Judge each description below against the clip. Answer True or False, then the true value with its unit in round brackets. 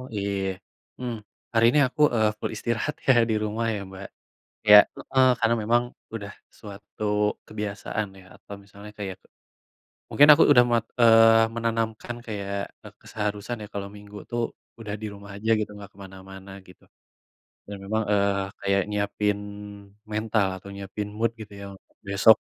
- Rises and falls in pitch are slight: True (2.1 semitones)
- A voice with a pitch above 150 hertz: False (105 Hz)